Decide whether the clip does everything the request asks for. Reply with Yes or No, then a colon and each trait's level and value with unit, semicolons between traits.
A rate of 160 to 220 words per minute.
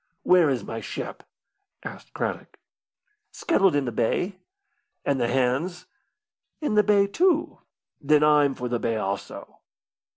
No: slow, 135 wpm